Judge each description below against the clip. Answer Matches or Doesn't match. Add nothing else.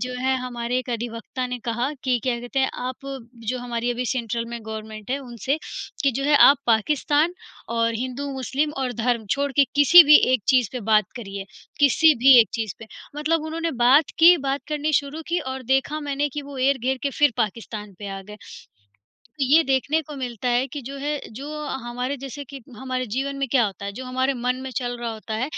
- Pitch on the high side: Matches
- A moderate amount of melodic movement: Matches